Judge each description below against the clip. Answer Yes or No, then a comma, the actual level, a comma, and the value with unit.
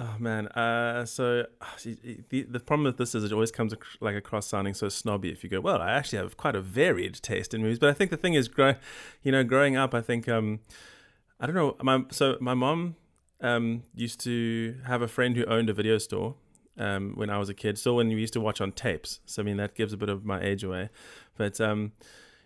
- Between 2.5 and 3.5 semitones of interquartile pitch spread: Yes, average, 2.8 semitones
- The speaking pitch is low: Yes, low, 115 Hz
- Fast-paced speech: Yes, fast, 240 wpm